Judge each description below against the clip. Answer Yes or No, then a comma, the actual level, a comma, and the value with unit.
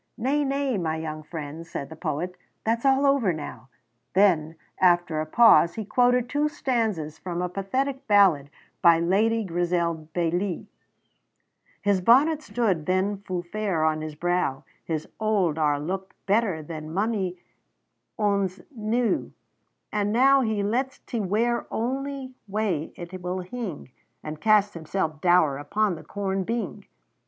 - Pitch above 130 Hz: Yes, high, 190 Hz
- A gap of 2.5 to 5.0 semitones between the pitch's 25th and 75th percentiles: No, wide, 5.6 semitones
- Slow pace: No, average, 145 wpm